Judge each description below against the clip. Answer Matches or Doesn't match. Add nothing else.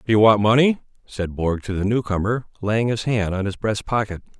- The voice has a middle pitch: Doesn't match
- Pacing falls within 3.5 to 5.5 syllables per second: Matches